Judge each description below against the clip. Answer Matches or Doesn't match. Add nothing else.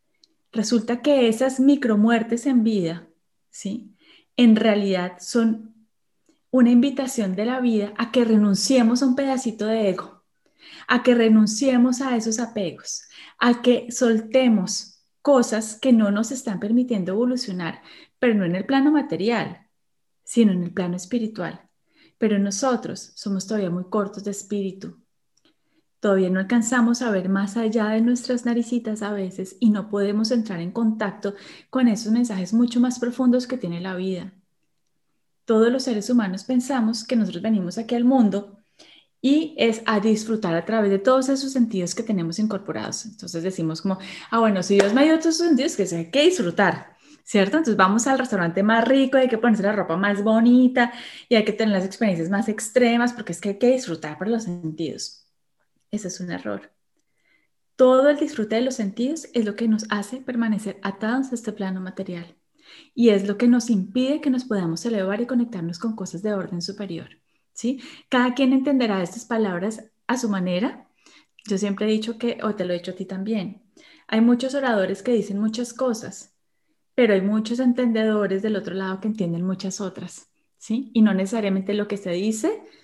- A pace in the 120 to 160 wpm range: Doesn't match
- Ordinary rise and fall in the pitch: Matches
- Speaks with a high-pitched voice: Matches